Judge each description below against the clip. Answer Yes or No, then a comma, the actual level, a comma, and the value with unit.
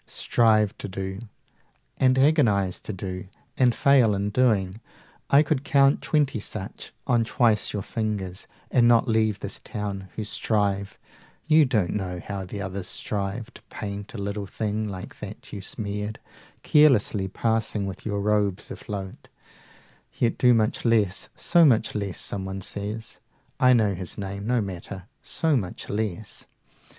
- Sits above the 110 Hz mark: No, low, 105 Hz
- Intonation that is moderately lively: Yes, average, 3.1 semitones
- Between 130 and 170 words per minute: Yes, average, 155 wpm